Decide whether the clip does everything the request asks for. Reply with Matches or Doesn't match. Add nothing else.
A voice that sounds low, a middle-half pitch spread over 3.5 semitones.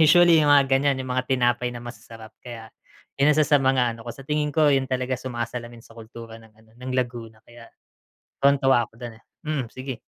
Doesn't match